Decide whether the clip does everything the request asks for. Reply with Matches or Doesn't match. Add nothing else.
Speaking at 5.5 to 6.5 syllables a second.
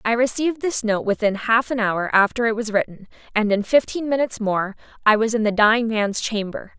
Matches